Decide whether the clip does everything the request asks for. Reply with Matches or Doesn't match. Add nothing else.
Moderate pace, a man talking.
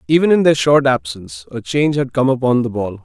Doesn't match